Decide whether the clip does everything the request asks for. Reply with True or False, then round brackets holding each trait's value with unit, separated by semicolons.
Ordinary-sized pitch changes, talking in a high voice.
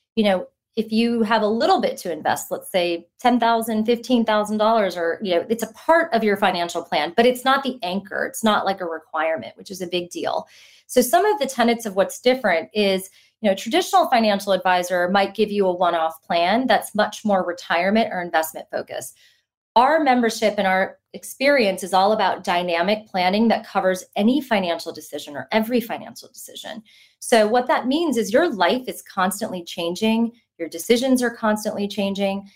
True (4.0 semitones; 210 Hz)